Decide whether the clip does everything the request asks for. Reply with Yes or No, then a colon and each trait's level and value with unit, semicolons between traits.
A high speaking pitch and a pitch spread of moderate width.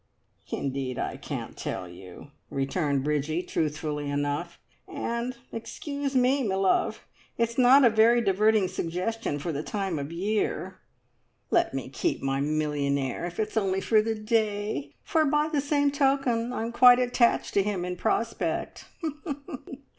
No: high, 205 Hz; wide, 7.9 semitones